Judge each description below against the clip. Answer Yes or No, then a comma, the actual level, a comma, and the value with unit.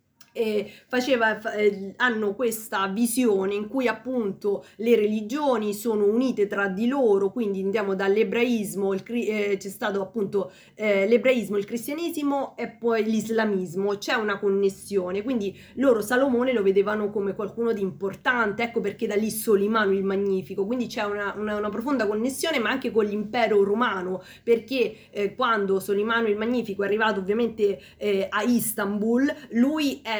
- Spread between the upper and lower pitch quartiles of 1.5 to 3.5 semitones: Yes, average, 2.8 semitones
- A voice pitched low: No, high, 215 Hz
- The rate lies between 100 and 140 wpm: No, average, 155 wpm